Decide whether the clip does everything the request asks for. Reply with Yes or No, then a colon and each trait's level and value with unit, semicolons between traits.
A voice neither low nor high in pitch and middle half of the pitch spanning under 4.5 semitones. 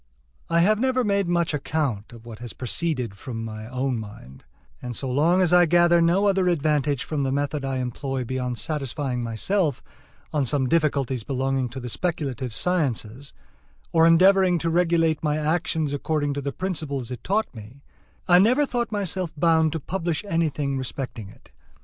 No: medium, 145 Hz; average, 5.1 semitones